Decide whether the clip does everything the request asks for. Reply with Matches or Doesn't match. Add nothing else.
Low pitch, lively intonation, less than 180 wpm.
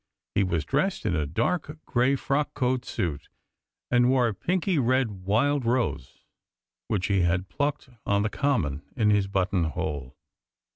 Matches